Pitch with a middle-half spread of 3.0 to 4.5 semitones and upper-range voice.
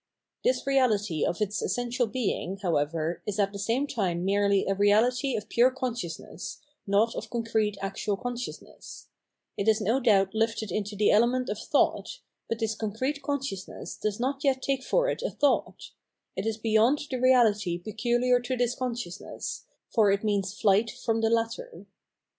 Yes: average, 3.7 semitones; high, 225 Hz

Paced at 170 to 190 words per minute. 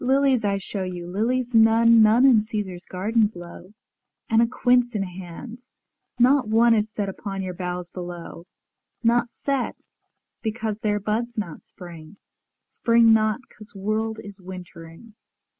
No: average, 140 wpm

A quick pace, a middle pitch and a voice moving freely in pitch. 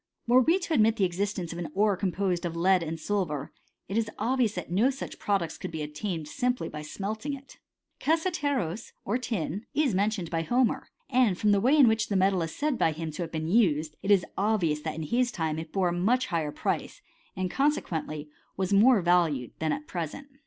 No: fast, 215 wpm; high, 195 Hz; wide, 6.2 semitones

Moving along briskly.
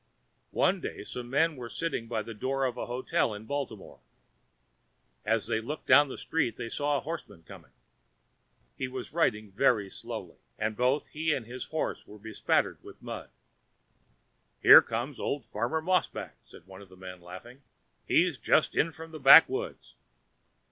No: average, 165 wpm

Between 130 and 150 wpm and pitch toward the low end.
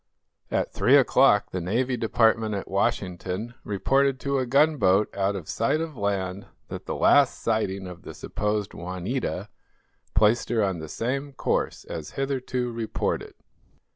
Yes: average, 145 wpm; low, 110 Hz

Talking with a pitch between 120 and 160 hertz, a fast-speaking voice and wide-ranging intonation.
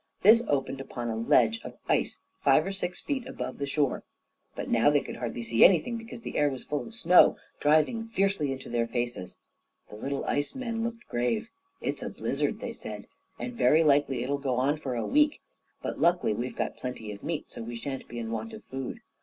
Yes: medium, 140 Hz; fast, 215 wpm; wide, 8.0 semitones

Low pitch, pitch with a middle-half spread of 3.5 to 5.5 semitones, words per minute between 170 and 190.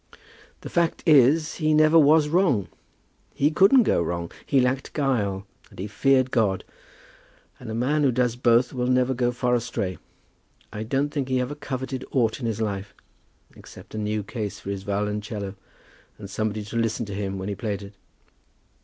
Yes: low, 120 Hz; average, 4.7 semitones; average, 180 wpm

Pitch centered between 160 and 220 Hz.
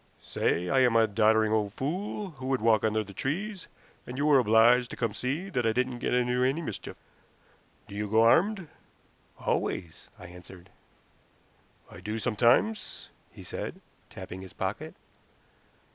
No: low, 120 Hz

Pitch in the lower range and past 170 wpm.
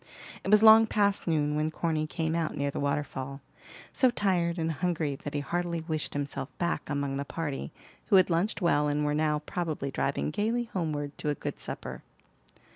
No: medium, 155 Hz; average, 190 wpm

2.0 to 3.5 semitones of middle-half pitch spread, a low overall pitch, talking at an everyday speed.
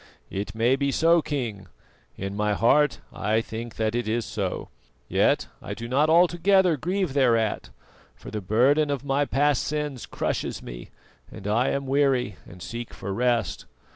No: average, 5.0 semitones; low, 125 Hz; average, 165 wpm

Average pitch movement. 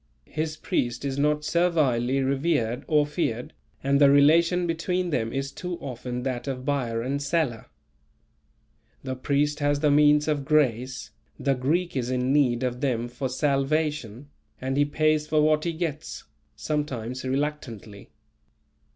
Yes: average, 3.1 semitones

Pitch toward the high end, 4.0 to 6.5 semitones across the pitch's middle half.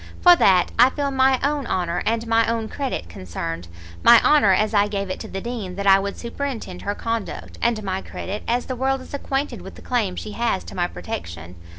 Yes: high, 220 Hz; average, 4.9 semitones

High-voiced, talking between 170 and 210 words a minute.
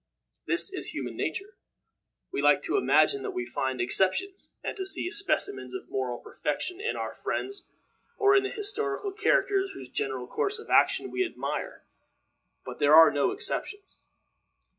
No: very high, 385 Hz; average, 160 wpm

